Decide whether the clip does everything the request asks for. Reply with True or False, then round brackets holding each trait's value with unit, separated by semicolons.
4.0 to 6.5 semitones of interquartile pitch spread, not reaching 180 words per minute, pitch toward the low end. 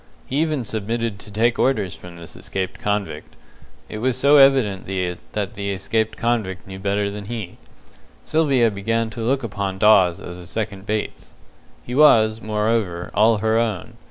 False (2.9 semitones; 160 wpm; 110 Hz)